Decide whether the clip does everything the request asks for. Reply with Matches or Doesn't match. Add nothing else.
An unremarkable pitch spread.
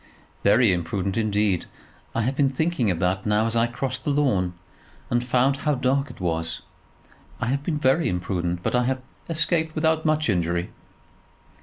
Doesn't match